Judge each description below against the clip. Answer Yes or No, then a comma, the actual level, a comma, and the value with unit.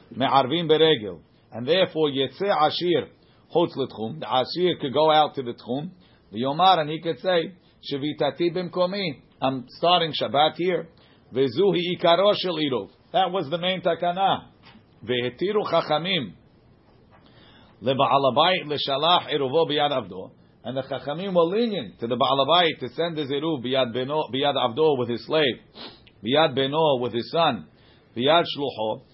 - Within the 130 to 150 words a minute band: Yes, average, 140 wpm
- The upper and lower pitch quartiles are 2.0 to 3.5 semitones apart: No, average, 4.7 semitones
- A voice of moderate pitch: Yes, medium, 150 Hz